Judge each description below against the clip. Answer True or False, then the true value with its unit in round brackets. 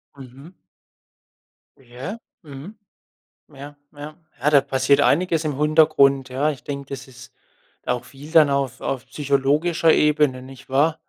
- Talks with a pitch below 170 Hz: True (140 Hz)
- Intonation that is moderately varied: False (2.3 semitones)